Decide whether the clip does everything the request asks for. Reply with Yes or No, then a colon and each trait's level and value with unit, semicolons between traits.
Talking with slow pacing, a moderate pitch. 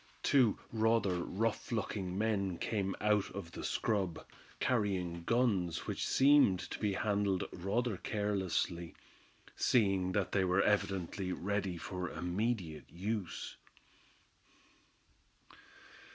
No: slow, 105 wpm; low, 100 Hz